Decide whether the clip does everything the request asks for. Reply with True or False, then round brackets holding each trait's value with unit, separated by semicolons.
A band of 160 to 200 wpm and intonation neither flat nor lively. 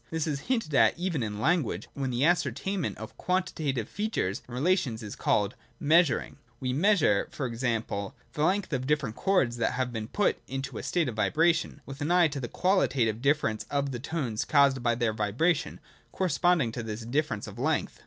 False (185 wpm; 6.1 semitones)